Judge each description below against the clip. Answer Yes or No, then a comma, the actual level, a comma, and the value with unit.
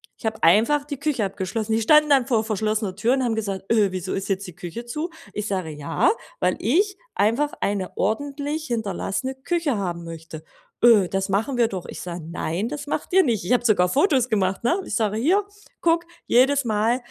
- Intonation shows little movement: No, wide, 6.2 semitones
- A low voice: No, high, 220 Hz